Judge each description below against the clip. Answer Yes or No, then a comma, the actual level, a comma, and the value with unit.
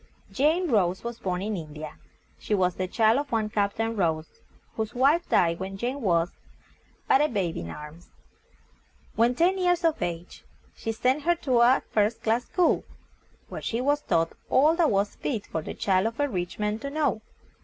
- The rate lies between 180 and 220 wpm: Yes, average, 195 wpm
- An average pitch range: No, wide, 7.1 semitones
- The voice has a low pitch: No, high, 220 Hz